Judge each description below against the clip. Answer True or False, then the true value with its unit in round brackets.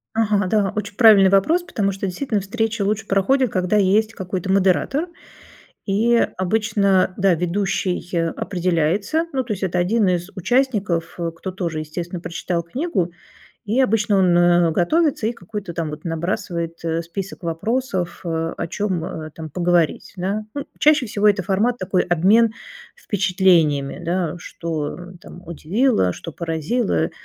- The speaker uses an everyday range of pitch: True (3.8 semitones)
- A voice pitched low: False (190 Hz)